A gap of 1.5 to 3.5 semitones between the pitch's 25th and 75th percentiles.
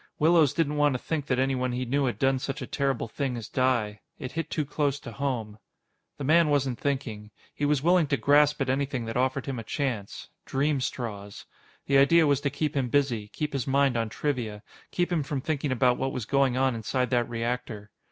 Yes: average, 2.8 semitones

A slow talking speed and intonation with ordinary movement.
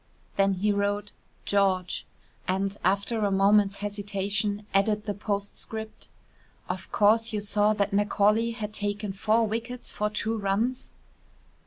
No: slow, 130 wpm; narrow, 1.2 semitones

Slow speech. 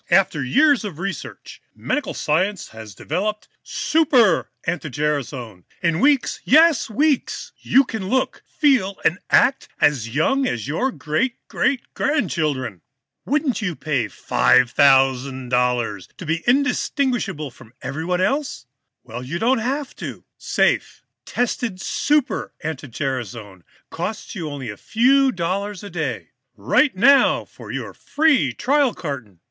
Yes: slow, 130 wpm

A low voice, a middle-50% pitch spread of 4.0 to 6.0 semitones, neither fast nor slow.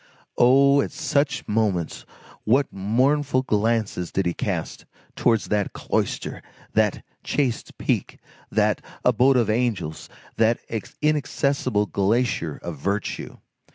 No: low, 115 Hz; average, 4.8 semitones; slow, 110 wpm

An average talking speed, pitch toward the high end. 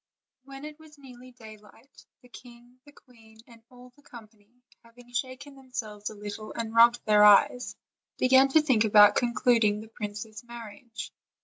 Yes: average, 155 wpm; high, 235 Hz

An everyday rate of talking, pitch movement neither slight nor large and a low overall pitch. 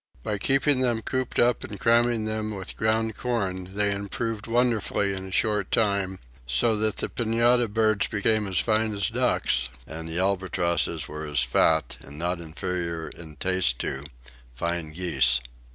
Yes: average, 160 wpm; average, 4.7 semitones; low, 100 Hz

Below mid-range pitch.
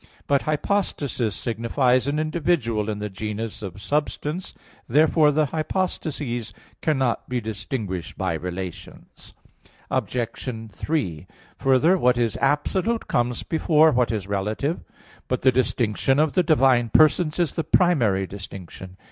Yes: low, 125 Hz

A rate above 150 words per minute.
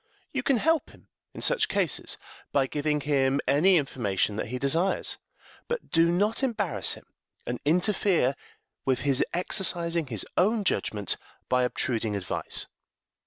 No: average, 140 wpm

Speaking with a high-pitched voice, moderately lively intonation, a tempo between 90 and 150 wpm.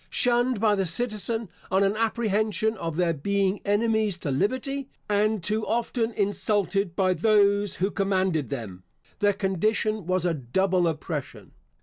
Yes: high, 200 Hz; average, 3.0 semitones; average, 140 wpm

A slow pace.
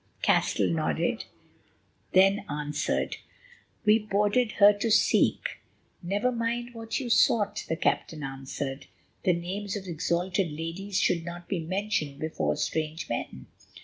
Yes: slow, 125 wpm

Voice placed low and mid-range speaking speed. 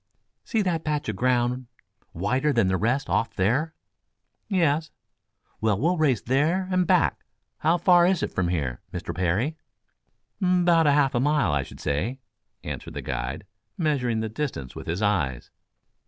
Yes: low, 130 Hz; average, 155 wpm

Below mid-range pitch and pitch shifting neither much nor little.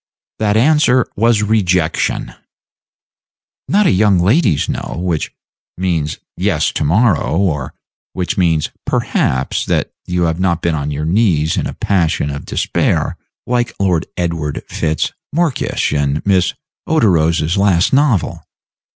Yes: very low, 90 Hz; average, 5.0 semitones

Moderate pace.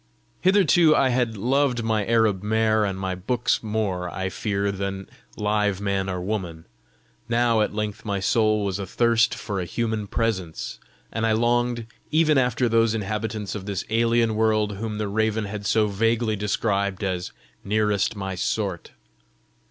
Yes: average, 155 wpm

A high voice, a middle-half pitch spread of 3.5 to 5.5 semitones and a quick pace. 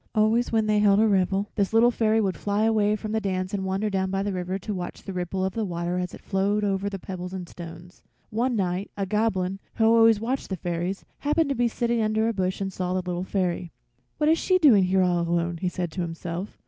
No: high, 195 Hz; average, 3.1 semitones; fast, 245 wpm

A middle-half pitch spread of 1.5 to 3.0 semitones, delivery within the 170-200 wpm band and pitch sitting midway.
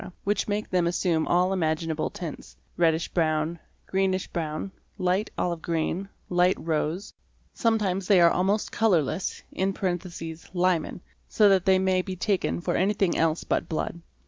No: average, 2.7 semitones; average, 145 wpm; medium, 180 Hz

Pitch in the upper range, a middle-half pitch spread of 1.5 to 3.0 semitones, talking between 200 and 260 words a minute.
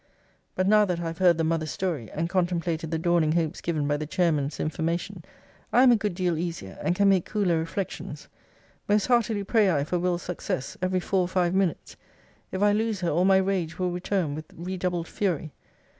No: medium, 175 Hz; average, 2.7 semitones; fast, 205 wpm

